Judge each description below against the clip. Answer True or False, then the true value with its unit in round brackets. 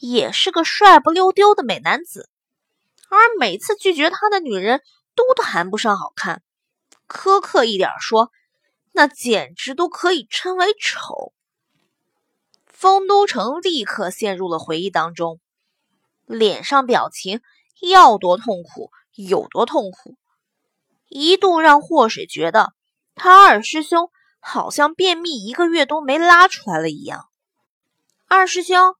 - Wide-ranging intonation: True (8.8 semitones)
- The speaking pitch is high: True (315 Hz)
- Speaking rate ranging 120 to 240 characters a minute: True (190 characters per minute)